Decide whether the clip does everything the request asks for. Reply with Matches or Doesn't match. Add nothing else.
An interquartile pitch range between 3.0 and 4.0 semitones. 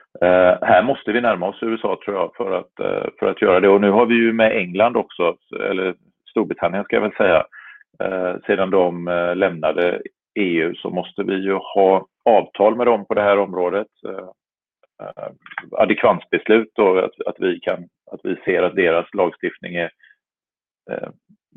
Matches